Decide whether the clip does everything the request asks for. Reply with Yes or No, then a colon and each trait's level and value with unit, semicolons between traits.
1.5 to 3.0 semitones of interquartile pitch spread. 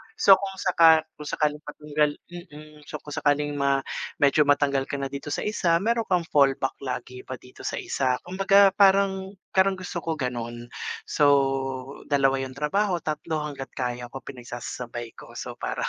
No: average, 4.8 semitones